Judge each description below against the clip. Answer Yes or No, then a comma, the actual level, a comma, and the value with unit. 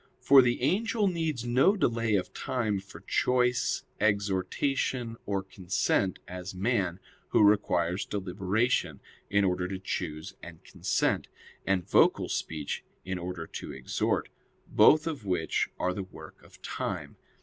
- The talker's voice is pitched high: No, low, 100 Hz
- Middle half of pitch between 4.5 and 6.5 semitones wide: Yes, average, 5.2 semitones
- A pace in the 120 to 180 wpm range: Yes, slow, 135 wpm